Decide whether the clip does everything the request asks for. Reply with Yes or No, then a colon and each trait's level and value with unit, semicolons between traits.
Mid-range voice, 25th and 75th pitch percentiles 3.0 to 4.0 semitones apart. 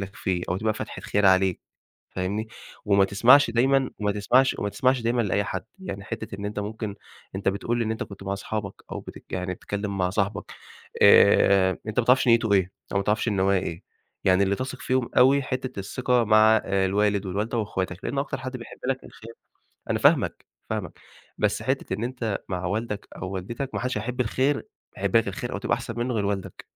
No: low, 105 Hz; average, 3.5 semitones